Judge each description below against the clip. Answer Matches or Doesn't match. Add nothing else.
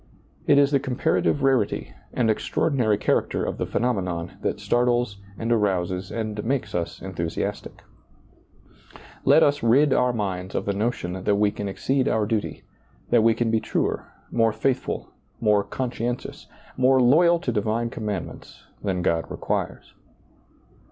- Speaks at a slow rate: Doesn't match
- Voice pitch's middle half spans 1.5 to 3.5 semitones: Doesn't match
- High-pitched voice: Doesn't match